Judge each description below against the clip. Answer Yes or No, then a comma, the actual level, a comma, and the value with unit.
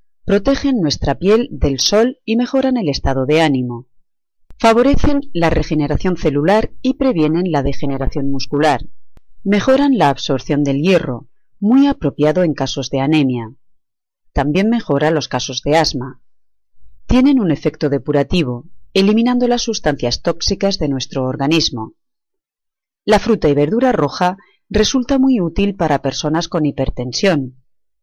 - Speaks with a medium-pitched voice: Yes, medium, 155 Hz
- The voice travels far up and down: Yes, wide, 7.7 semitones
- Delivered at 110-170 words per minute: Yes, average, 130 wpm